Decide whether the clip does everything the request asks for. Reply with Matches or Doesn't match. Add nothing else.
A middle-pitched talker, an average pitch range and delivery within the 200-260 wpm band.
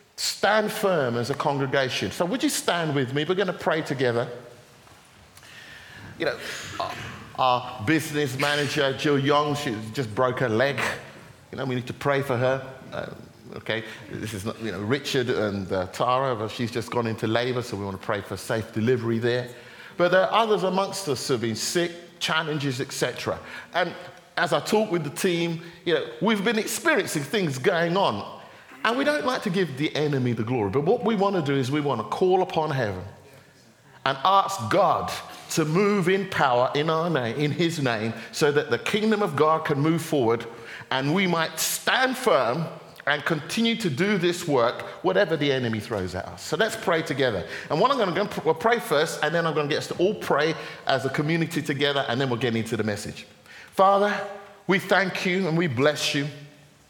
Doesn't match